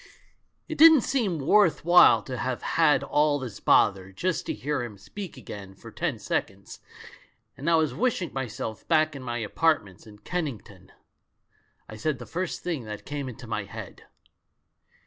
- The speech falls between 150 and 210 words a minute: Yes, average, 165 wpm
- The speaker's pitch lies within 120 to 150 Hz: Yes, medium, 140 Hz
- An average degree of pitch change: No, wide, 7.1 semitones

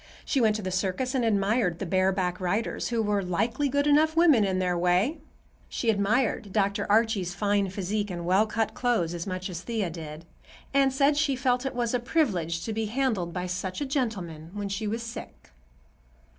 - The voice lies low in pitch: No, high, 205 Hz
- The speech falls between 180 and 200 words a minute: Yes, average, 195 wpm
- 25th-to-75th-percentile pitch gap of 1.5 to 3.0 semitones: No, average, 5.0 semitones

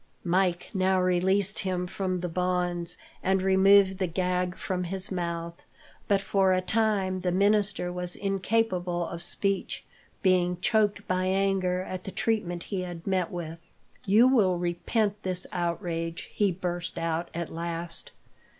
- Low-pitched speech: No, medium, 185 Hz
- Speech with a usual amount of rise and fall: No, narrow, 1.8 semitones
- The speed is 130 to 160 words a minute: Yes, average, 145 wpm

